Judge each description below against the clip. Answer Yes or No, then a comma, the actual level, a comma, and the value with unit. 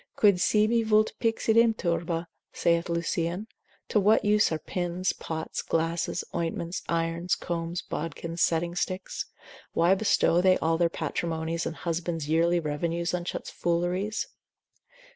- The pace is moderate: No, slow, 130 wpm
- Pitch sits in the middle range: Yes, medium, 170 Hz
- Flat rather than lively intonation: Yes, narrow, 2.1 semitones